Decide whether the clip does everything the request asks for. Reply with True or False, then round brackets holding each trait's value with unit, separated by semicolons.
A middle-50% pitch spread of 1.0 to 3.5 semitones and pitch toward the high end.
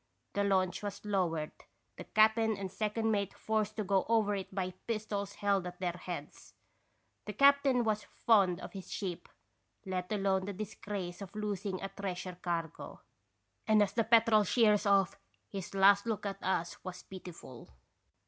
True (2.4 semitones; 200 Hz)